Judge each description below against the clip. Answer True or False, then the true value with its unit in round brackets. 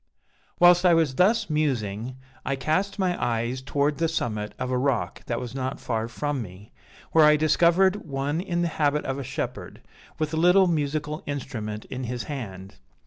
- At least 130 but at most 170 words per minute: False (180 wpm)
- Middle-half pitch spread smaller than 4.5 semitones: False (5.1 semitones)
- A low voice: False (145 Hz)